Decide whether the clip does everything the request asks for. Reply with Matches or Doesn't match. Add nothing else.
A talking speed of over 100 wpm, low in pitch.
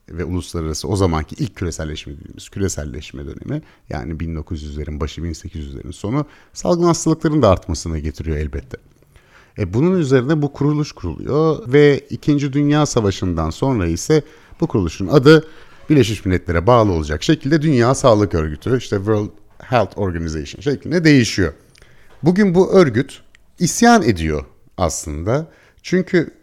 Matches